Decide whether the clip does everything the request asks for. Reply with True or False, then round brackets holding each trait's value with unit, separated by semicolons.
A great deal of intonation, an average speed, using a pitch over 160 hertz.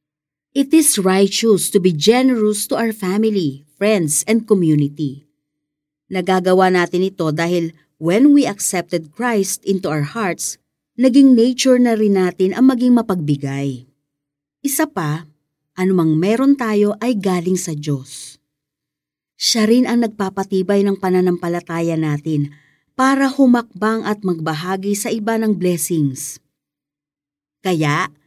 True (6.2 semitones; 120 wpm; 185 Hz)